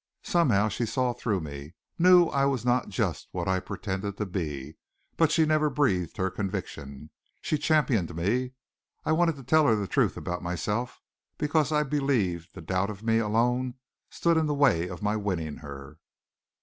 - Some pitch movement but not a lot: No, wide, 7.8 semitones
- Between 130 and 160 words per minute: No, average, 175 wpm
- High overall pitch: No, low, 110 Hz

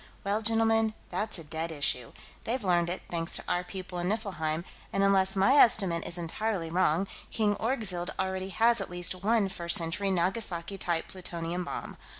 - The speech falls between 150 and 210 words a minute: Yes, average, 170 wpm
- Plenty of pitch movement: No, average, 3.5 semitones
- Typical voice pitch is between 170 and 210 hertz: Yes, medium, 185 Hz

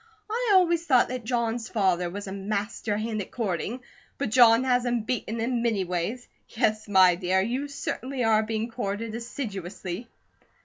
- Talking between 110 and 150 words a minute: No, average, 165 wpm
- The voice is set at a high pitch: Yes, high, 225 Hz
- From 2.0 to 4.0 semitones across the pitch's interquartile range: Yes, average, 3.7 semitones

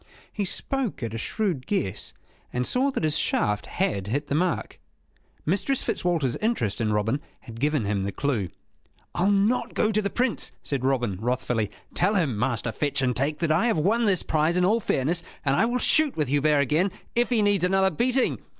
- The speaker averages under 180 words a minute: No, average, 195 wpm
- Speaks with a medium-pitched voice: Yes, medium, 155 Hz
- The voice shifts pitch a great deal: Yes, wide, 8.4 semitones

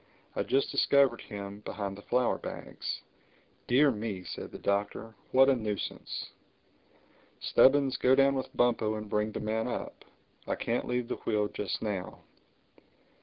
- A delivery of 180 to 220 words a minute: No, average, 150 wpm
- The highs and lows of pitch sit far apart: No, average, 3.7 semitones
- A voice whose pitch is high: No, low, 110 Hz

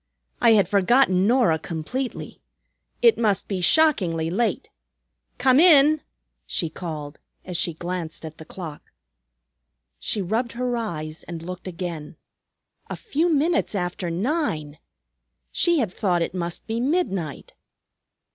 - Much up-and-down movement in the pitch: Yes, wide, 7.1 semitones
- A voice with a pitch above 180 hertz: Yes, high, 190 Hz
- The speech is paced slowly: Yes, slow, 130 wpm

